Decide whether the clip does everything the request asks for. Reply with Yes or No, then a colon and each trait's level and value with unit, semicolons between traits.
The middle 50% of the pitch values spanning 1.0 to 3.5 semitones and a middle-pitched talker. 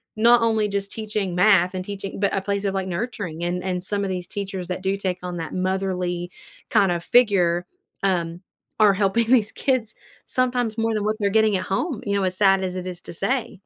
No: average, 2.9 semitones; high, 195 Hz